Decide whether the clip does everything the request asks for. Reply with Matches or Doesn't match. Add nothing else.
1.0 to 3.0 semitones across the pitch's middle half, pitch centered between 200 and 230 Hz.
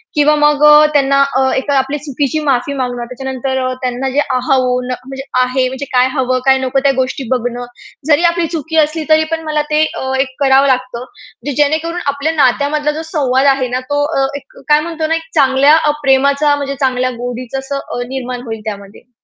Doesn't match